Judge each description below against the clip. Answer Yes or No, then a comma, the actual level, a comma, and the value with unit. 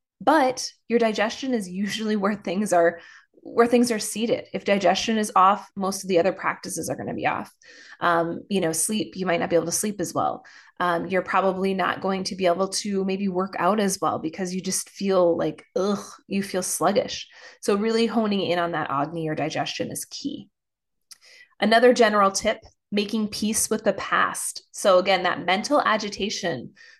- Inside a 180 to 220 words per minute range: Yes, average, 190 wpm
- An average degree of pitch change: Yes, average, 3.4 semitones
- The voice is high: Yes, high, 195 Hz